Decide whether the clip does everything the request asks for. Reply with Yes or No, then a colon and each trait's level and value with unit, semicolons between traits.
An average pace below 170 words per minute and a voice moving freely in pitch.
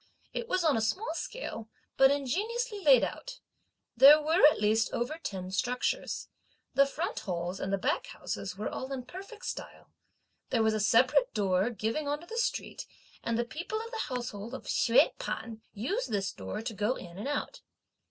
No: average, 185 wpm; wide, 8.0 semitones